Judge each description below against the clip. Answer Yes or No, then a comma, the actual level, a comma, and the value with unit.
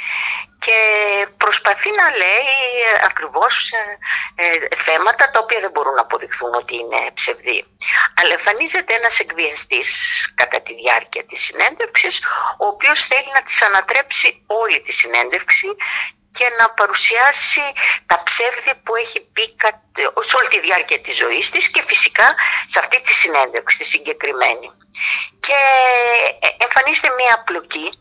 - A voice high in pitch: Yes, very high, 270 Hz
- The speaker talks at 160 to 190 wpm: No, average, 130 wpm